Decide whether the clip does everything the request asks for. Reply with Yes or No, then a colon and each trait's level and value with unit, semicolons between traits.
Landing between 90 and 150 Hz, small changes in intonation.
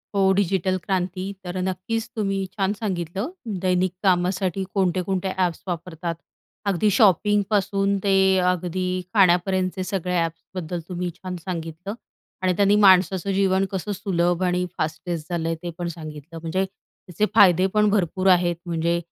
No: medium, 185 Hz; narrow, 2.0 semitones